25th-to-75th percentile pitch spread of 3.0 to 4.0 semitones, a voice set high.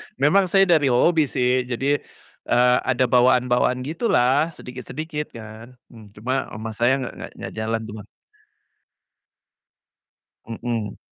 No: average, 3.7 semitones; low, 125 Hz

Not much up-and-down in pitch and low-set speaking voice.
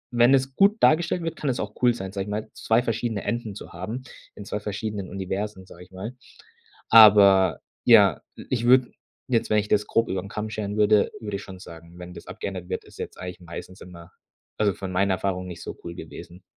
No: average, 3.6 semitones; low, 105 Hz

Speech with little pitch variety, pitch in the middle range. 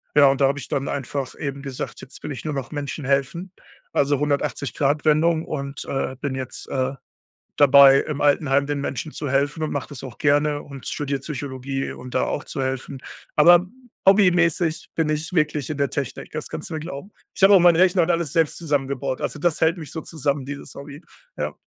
Yes: narrow, 2.3 semitones; medium, 145 Hz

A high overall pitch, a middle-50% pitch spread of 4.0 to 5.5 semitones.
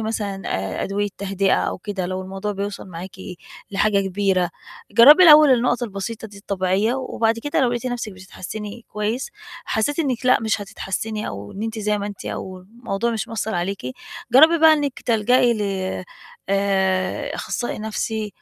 No: high, 210 Hz; average, 3.3 semitones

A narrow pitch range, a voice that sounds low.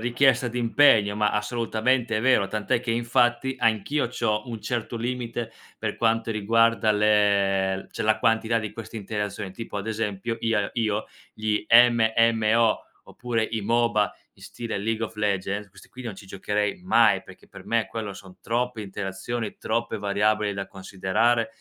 Yes: narrow, 2.2 semitones; low, 110 Hz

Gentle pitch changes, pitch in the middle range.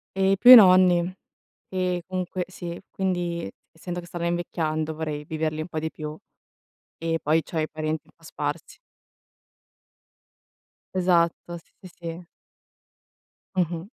Yes: narrow, 2.3 semitones; medium, 170 Hz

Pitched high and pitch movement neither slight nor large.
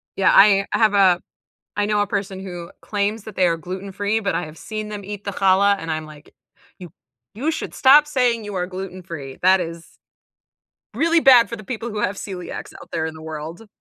Yes: high, 195 Hz; average, 3.3 semitones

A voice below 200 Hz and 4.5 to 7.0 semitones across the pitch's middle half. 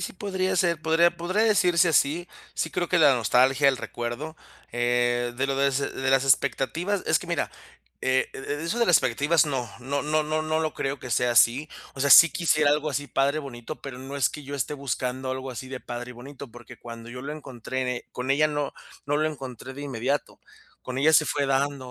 No: medium, 140 Hz; average, 3.3 semitones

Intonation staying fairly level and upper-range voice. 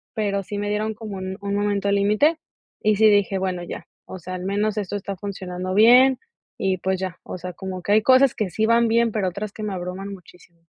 Yes: narrow, 2.3 semitones; high, 200 Hz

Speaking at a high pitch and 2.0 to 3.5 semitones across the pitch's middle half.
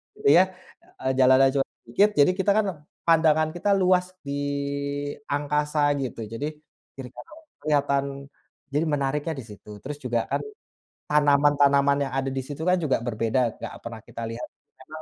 No: medium, 145 Hz; average, 2.8 semitones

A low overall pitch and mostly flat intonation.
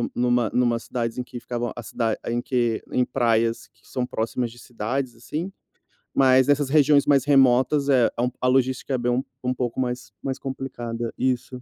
Yes: low, 125 Hz; narrow, 1.8 semitones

